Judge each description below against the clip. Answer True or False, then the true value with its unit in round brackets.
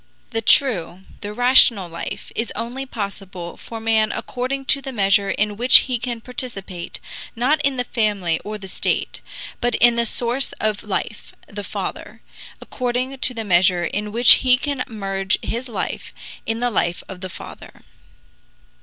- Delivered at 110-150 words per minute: False (165 wpm)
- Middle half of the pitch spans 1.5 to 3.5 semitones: False (4.1 semitones)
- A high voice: True (225 Hz)